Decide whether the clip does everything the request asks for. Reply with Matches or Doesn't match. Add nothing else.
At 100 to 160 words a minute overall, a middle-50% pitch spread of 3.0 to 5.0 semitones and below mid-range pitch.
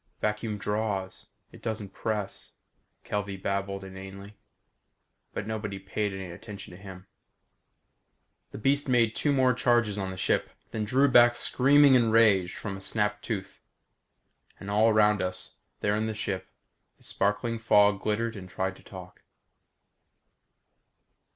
Doesn't match